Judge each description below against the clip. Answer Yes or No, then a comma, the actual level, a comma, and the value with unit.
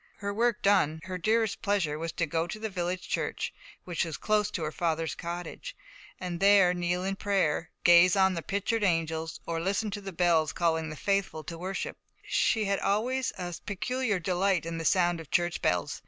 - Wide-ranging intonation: No, average, 3.3 semitones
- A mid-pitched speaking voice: Yes, medium, 180 Hz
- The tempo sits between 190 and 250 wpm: Yes, average, 195 wpm